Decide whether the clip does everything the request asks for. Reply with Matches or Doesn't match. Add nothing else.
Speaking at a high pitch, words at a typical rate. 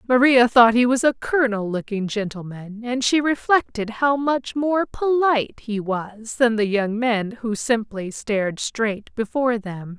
Matches